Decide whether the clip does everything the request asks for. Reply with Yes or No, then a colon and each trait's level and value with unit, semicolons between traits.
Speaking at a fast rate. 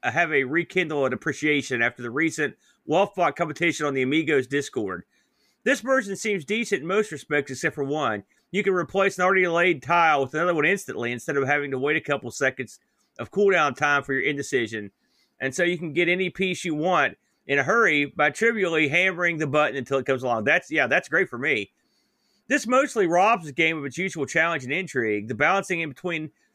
Yes: fast, 210 wpm